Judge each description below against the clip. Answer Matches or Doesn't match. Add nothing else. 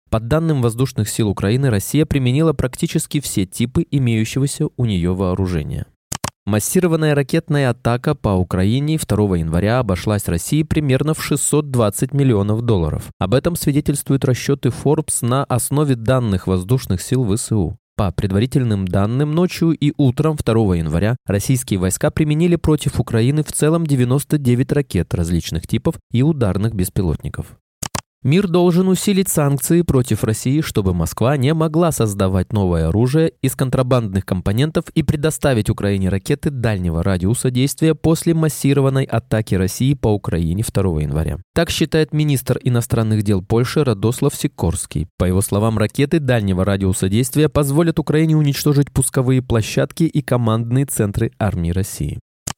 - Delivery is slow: Doesn't match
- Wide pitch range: Matches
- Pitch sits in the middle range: Doesn't match